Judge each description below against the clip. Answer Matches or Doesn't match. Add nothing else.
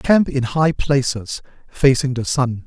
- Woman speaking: Doesn't match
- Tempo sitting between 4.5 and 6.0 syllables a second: Doesn't match